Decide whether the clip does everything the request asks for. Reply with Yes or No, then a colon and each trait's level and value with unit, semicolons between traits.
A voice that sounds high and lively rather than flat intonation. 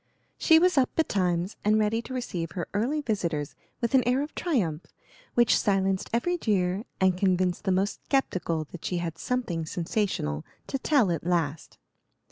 Yes: high, 195 Hz; wide, 6.0 semitones